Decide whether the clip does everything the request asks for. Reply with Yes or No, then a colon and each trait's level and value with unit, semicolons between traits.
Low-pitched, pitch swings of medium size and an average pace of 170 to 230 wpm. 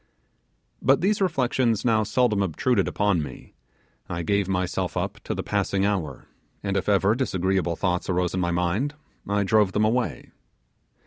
No: low, 100 Hz; average, 4.2 semitones; average, 155 wpm